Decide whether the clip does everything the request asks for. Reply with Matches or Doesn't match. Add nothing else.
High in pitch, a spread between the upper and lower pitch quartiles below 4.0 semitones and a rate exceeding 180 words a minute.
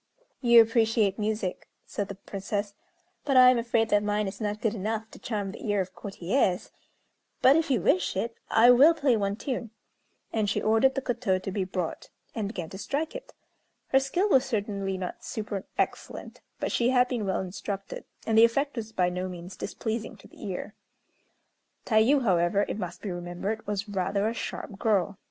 Matches